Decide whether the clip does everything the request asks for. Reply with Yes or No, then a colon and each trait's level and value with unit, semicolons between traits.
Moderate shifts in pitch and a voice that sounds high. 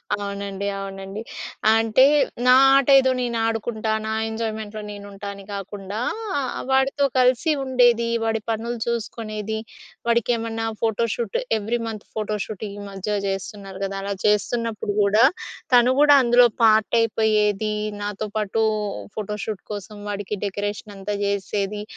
No: narrow, 2.2 semitones; high, 215 Hz